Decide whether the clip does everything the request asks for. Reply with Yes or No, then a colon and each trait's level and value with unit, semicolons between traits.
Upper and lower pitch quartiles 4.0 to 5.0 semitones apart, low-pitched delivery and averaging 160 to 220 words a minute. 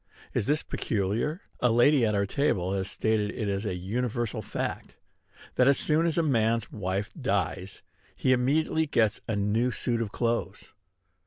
Yes: average, 4.3 semitones; low, 115 Hz; average, 165 wpm